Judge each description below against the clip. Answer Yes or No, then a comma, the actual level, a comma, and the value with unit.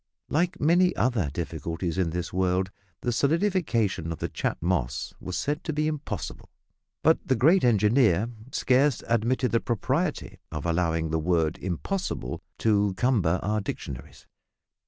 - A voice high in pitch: No, low, 105 Hz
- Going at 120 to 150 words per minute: Yes, average, 140 wpm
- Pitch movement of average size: No, wide, 8.2 semitones